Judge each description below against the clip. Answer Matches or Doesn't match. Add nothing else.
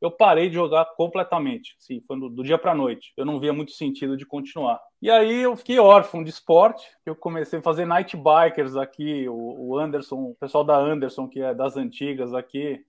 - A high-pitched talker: Doesn't match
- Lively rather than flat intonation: Doesn't match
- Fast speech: Matches